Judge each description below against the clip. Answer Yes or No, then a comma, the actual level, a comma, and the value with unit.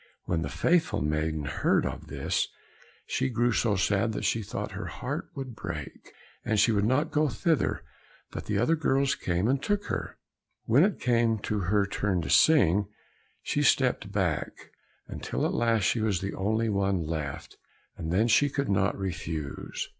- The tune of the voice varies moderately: No, wide, 5.8 semitones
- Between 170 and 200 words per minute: Yes, average, 175 wpm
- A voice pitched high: No, low, 105 Hz